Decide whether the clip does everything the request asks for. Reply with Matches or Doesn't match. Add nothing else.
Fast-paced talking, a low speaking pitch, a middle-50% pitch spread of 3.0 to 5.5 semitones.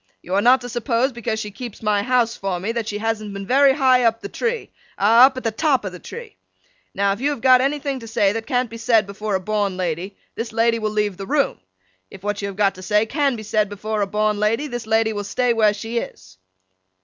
Doesn't match